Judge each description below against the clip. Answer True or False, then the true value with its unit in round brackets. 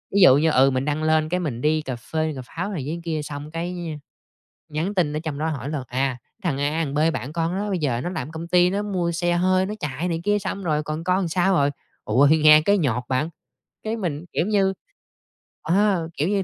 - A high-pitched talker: False (160 Hz)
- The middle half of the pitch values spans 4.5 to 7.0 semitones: False (3.8 semitones)